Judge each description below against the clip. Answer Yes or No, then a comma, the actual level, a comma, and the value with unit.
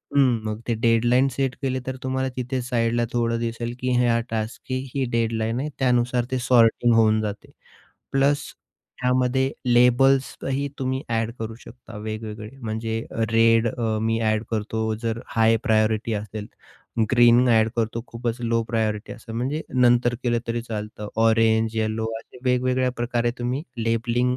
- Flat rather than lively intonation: Yes, narrow, 2.0 semitones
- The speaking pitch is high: No, low, 115 Hz